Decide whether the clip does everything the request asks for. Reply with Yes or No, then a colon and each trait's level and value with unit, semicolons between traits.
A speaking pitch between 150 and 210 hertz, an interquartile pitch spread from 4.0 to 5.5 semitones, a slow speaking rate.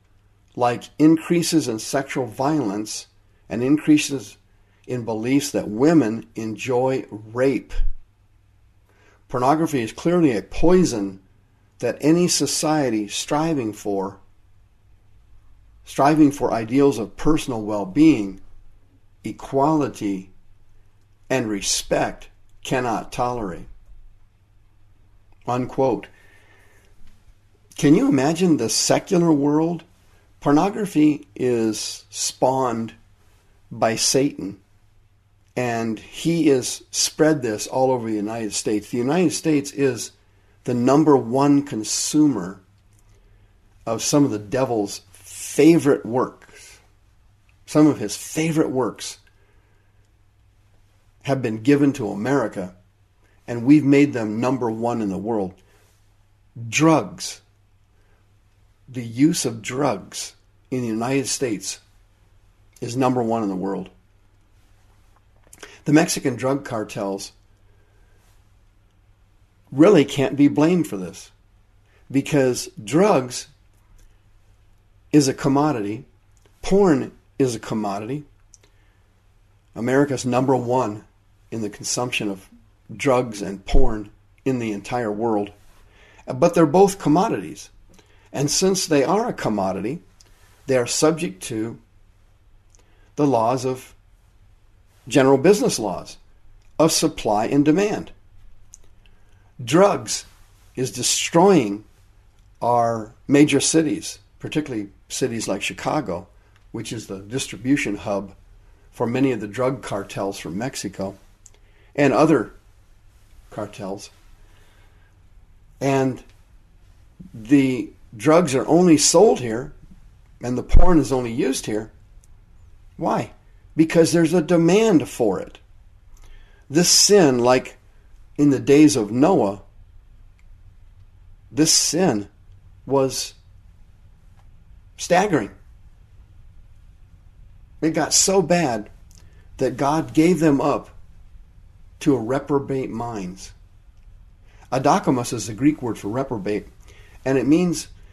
No: low, 105 Hz; average, 5.1 semitones; slow, 100 wpm